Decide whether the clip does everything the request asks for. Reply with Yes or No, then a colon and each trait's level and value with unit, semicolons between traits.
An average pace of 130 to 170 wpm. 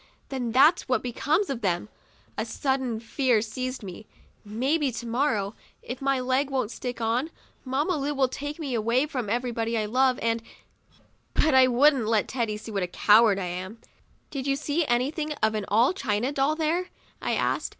No: average, 185 wpm